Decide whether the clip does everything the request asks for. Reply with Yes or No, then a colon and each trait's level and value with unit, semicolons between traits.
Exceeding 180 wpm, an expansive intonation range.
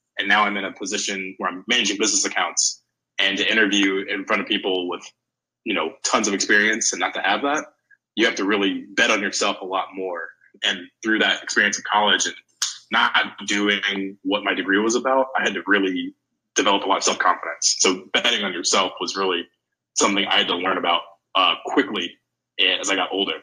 Yes: fast, 205 wpm; wide, 6.6 semitones